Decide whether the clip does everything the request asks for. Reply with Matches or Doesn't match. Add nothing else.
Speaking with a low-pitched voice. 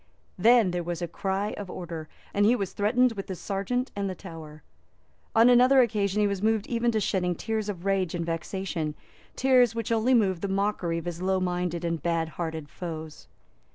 Doesn't match